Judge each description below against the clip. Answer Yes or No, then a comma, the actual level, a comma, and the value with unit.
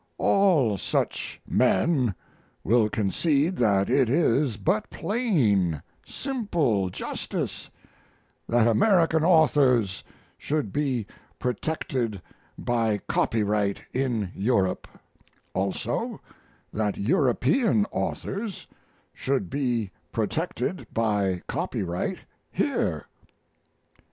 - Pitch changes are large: Yes, wide, 7.1 semitones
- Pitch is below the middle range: Yes, low, 120 Hz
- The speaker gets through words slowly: Yes, slow, 80 wpm